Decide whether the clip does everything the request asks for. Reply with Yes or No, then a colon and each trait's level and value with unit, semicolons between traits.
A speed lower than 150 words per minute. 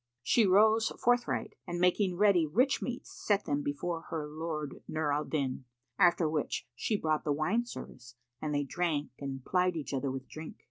No: average, 180 wpm